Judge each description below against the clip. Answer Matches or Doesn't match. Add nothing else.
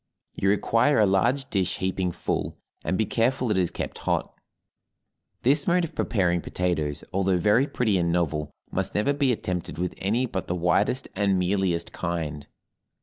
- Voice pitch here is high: Doesn't match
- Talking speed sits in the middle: Matches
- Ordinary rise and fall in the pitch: Matches